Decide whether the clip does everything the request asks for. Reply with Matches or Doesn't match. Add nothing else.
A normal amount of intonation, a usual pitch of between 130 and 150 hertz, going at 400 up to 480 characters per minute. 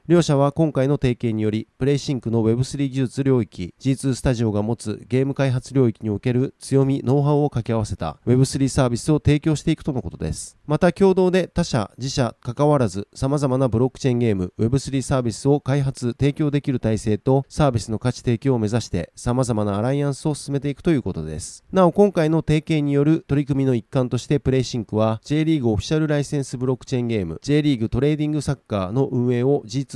Matches